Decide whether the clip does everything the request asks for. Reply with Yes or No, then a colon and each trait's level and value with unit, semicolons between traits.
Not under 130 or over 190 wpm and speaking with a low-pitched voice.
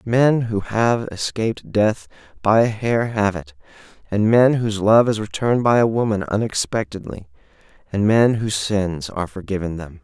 Yes: average, 160 wpm; low, 105 Hz